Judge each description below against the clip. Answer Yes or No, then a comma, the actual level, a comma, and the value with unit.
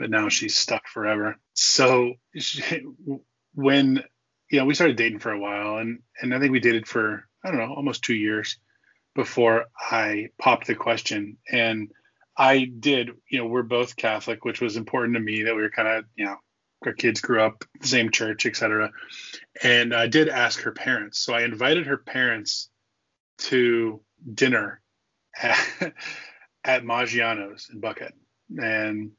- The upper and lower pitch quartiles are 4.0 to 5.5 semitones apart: No, average, 3.0 semitones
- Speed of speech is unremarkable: Yes, average, 170 wpm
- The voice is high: No, low, 120 Hz